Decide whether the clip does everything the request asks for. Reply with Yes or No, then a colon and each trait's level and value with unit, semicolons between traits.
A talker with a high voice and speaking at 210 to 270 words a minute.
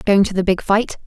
No: high, 200 Hz; fast, 285 wpm